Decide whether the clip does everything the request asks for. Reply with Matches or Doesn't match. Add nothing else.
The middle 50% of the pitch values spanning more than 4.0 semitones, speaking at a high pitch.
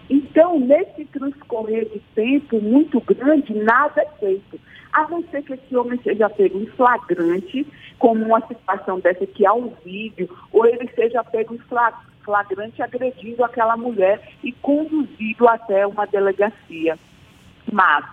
Matches